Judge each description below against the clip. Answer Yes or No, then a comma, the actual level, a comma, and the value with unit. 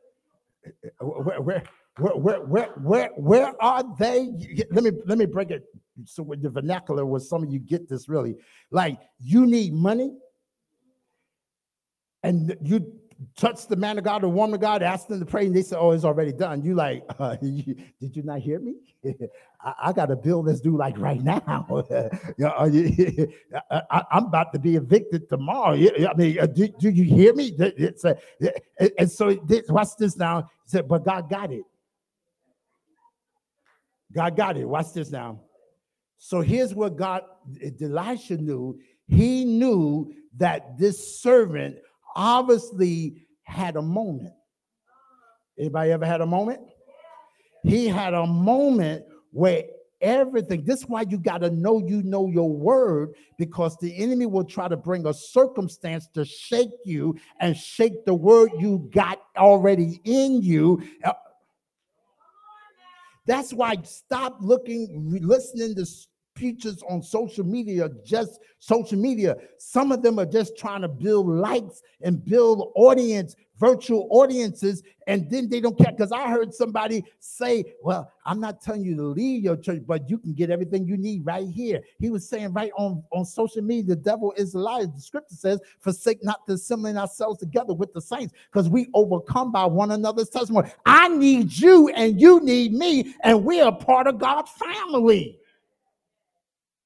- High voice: Yes, high, 200 Hz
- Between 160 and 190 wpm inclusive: Yes, average, 165 wpm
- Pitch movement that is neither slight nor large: No, wide, 5.7 semitones